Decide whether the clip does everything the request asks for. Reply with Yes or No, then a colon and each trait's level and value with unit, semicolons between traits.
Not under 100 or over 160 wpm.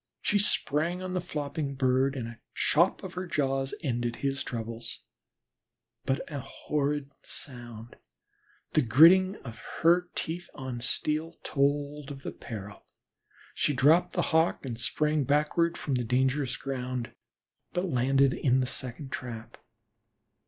Yes: average, 140 wpm